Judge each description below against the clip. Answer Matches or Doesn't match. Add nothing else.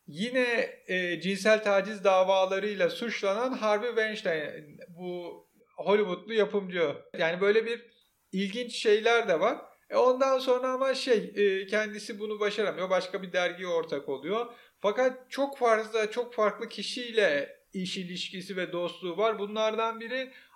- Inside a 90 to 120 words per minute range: Doesn't match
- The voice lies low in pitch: Doesn't match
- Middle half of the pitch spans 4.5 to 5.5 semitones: Doesn't match